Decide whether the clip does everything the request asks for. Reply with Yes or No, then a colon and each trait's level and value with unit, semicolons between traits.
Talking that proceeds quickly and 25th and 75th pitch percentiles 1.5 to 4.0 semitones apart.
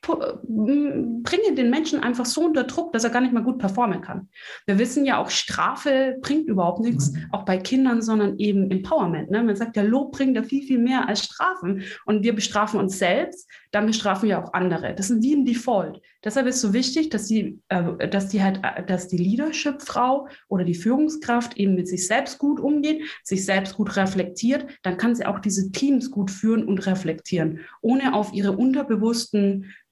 No: fast, 195 wpm; average, 5.2 semitones